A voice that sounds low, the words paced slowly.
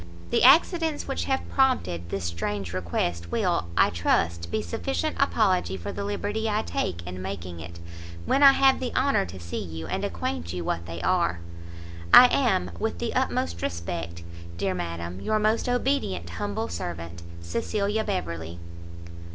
No: very low, 90 Hz; average, 160 wpm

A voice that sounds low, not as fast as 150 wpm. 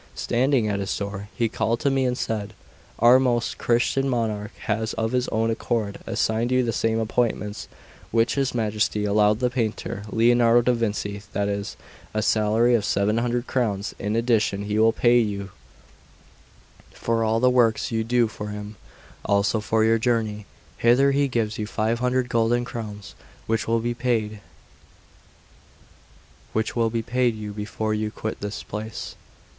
No: low, 115 Hz; average, 155 wpm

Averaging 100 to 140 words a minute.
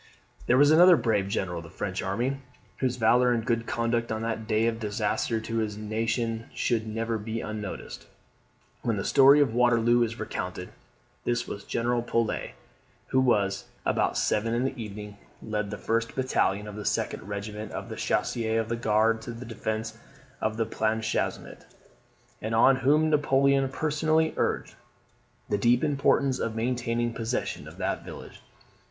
No: average, 160 wpm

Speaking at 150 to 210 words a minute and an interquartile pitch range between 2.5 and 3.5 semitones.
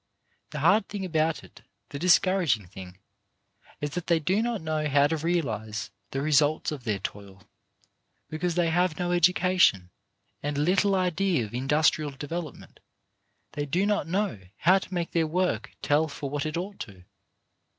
No: average, 165 wpm; average, 4.2 semitones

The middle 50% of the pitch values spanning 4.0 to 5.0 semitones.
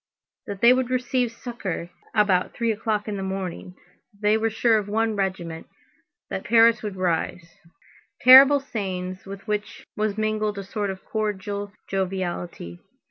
No: average, 2.9 semitones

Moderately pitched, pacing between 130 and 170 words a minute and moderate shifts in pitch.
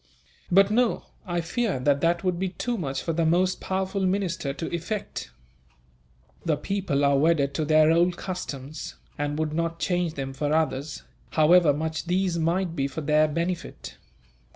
Yes: medium, 165 Hz; average, 165 wpm; average, 3.3 semitones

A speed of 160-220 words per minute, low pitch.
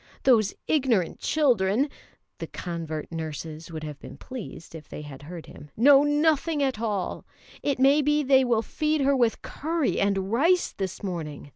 No: average, 165 wpm; high, 225 Hz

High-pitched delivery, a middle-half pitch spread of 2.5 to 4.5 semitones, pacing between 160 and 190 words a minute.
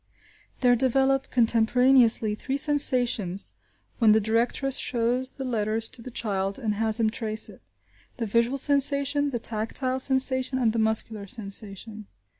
No: high, 235 Hz; average, 3.2 semitones; average, 140 wpm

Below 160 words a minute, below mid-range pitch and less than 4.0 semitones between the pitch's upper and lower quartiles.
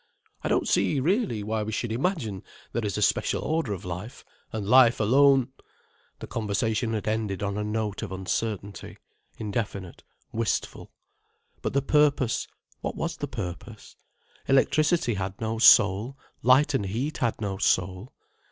No: average, 150 wpm; low, 110 Hz; average, 4.4 semitones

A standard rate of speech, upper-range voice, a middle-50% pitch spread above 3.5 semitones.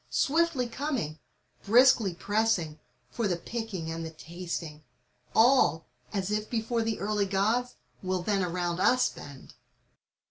No: slow, 130 wpm; high, 205 Hz; average, 5.3 semitones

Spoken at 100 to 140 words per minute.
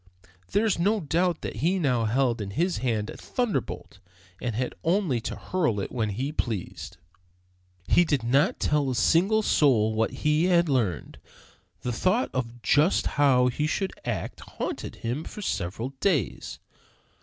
No: average, 160 wpm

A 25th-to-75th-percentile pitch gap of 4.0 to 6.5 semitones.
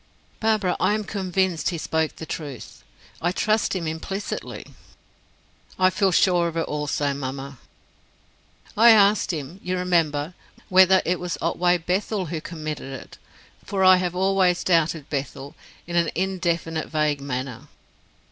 No: average, 3.5 semitones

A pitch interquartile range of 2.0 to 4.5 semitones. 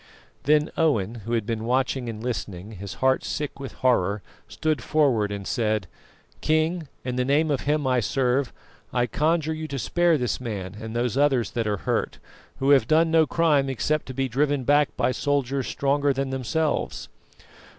Yes: average, 4.1 semitones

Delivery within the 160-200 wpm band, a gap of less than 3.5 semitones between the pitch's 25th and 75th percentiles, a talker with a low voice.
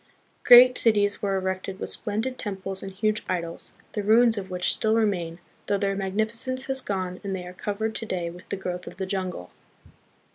No: average, 190 wpm; average, 2.8 semitones; high, 195 Hz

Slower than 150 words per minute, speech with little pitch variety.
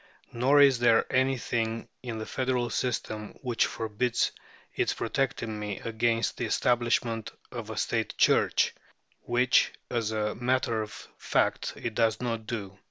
Yes: average, 140 wpm; narrow, 2.0 semitones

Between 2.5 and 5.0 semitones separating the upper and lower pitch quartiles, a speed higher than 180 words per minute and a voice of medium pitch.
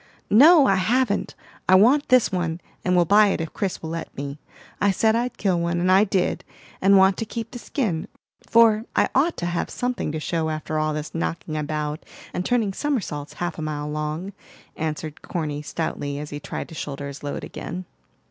No: wide, 5.6 semitones; average, 200 wpm; medium, 175 Hz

